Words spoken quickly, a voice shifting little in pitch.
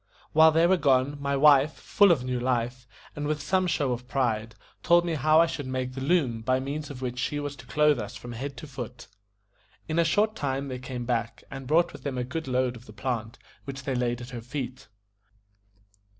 No: fast, 220 wpm; average, 3.4 semitones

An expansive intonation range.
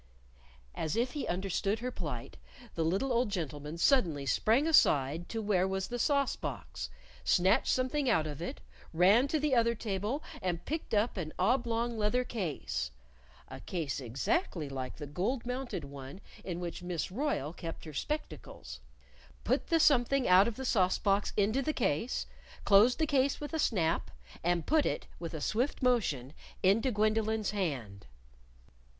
Yes: wide, 7.0 semitones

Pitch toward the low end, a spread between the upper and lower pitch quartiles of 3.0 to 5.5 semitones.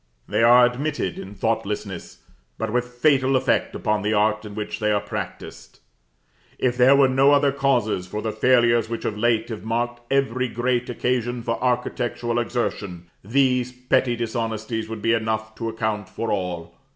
No: low, 115 Hz; narrow, 2.6 semitones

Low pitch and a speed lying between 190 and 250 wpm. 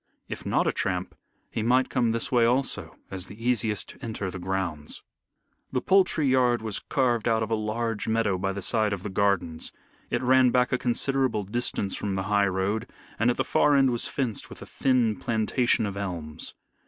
Yes: low, 110 Hz; average, 200 wpm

